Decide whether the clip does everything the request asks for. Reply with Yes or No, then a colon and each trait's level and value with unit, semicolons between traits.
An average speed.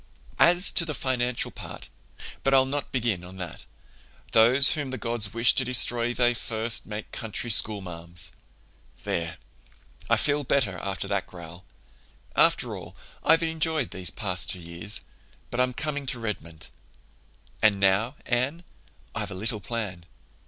Yes: average, 145 wpm